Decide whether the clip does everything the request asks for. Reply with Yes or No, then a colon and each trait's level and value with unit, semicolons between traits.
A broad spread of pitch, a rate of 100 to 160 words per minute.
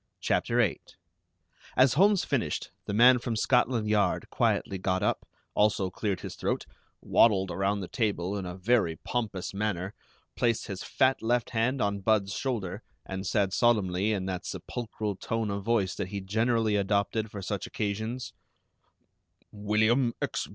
No: average, 3.3 semitones; average, 150 wpm